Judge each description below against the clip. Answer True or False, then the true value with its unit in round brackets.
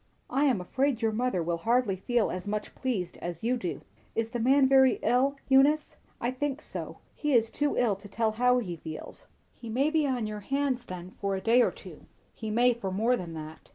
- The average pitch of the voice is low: False (235 Hz)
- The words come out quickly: True (220 wpm)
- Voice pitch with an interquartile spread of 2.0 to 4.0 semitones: False (4.8 semitones)